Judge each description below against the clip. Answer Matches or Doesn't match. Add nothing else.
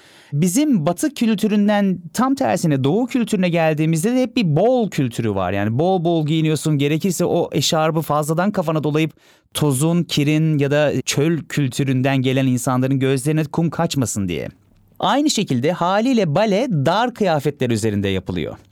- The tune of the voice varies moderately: Doesn't match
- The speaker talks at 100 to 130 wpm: Doesn't match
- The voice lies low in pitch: Doesn't match